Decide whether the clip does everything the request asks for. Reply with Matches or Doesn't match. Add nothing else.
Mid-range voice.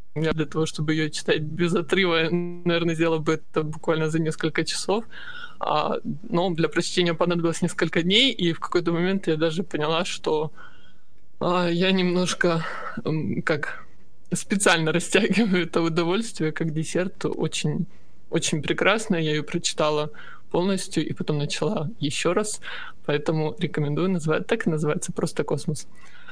Matches